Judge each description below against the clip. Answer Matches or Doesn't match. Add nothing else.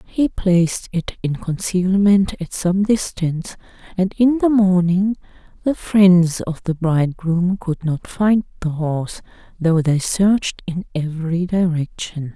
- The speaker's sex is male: Doesn't match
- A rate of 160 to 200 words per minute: Doesn't match